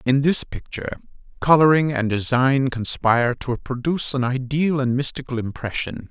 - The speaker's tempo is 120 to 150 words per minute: Yes, average, 140 wpm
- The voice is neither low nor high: No, low, 130 Hz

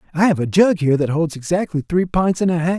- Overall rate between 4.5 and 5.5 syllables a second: No, 6.4 syllables/s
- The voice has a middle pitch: Yes, medium, 170 Hz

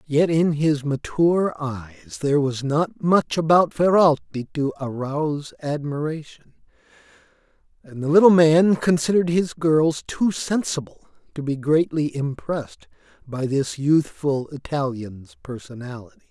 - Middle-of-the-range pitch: Yes, medium, 145 Hz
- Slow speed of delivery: Yes, slow, 120 wpm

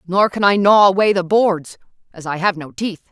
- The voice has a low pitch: No, medium, 185 Hz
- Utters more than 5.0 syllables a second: No, 4.9 syllables/s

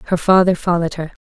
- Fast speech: No, average, 195 wpm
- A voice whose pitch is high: No, medium, 175 Hz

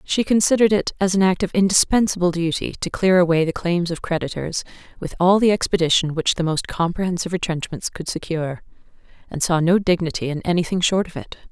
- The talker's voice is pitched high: No, medium, 175 Hz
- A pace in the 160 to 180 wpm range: No, average, 190 wpm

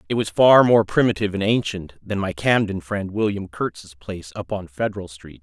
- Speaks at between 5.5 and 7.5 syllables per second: No, 5.2 syllables/s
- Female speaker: No, male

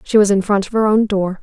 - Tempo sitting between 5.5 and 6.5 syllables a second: Yes, 6.0 syllables/s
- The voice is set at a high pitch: Yes, high, 205 Hz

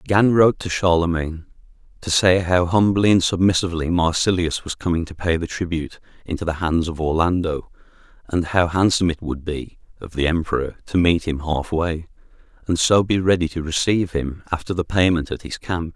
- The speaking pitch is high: No, very low, 85 Hz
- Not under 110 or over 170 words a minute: No, average, 180 wpm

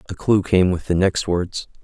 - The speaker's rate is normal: No, fast, 230 wpm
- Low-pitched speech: Yes, very low, 90 Hz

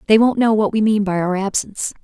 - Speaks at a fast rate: Yes, fast, 265 wpm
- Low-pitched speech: No, high, 210 Hz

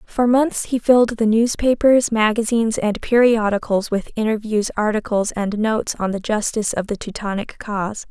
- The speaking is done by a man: No, female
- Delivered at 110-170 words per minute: Yes, average, 155 wpm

